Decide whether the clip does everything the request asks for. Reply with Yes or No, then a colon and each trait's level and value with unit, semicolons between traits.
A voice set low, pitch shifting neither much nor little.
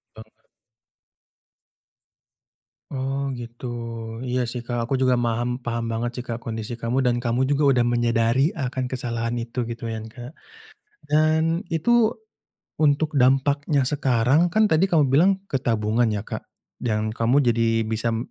Yes: low, 125 Hz; average, 3.2 semitones